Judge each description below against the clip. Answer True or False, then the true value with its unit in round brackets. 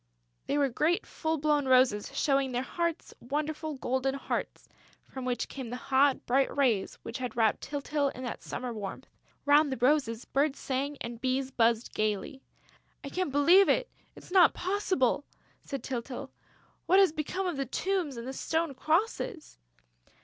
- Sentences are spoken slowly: False (165 wpm)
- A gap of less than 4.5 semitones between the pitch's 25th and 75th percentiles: True (3.5 semitones)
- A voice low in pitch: False (275 Hz)